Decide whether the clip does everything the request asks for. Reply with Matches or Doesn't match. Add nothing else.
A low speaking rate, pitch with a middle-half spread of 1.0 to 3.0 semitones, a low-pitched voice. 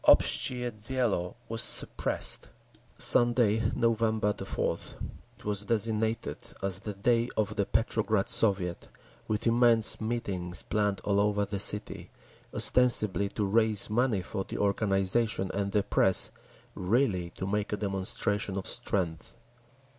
Matches